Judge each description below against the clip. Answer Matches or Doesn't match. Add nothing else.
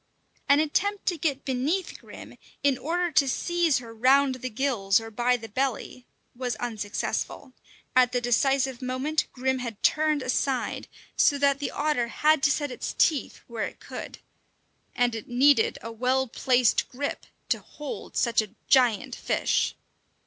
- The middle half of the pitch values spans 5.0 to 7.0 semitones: Doesn't match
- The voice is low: Doesn't match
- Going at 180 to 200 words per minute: Doesn't match